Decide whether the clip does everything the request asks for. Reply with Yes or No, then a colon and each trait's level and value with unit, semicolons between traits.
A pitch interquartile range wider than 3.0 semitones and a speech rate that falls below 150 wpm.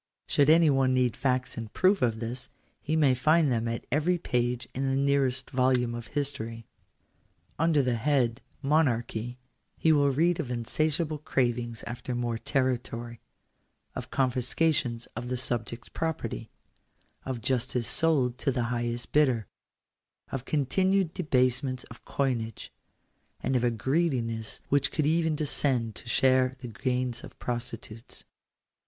Yes: average, 3.4 semitones; average, 140 wpm